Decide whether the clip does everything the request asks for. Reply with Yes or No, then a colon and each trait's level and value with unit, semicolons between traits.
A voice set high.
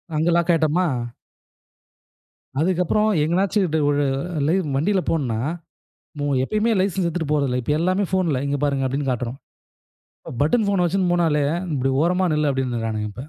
No: medium, 160 Hz